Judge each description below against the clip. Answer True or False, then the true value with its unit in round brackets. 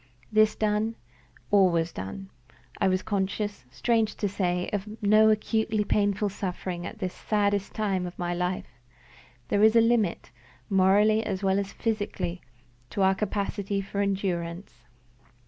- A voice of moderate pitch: False (200 Hz)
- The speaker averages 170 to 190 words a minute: False (145 wpm)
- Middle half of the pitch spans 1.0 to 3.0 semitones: True (2.4 semitones)